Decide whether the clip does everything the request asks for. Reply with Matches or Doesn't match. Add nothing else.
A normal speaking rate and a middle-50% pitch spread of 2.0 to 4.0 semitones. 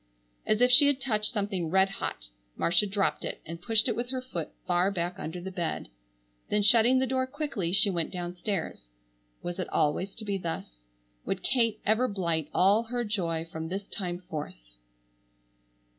Doesn't match